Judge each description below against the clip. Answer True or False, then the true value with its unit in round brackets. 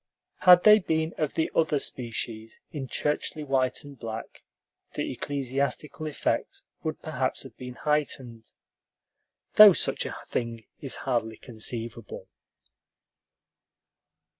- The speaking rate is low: True (115 wpm)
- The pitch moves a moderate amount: True (4.5 semitones)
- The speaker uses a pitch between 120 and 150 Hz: True (135 Hz)